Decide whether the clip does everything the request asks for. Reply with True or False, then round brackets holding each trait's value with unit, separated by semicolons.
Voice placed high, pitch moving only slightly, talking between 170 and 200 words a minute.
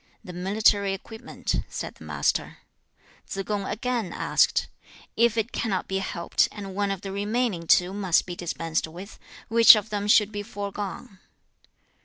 False (200 Hz; 2.2 semitones; 160 wpm)